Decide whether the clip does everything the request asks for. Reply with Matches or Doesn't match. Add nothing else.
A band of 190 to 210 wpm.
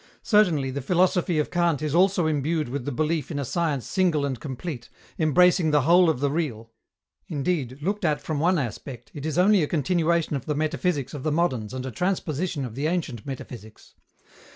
Matches